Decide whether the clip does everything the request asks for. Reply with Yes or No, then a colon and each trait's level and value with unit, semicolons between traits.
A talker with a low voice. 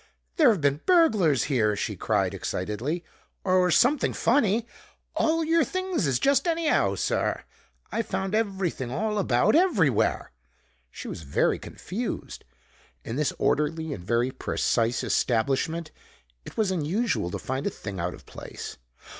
No: medium, 175 Hz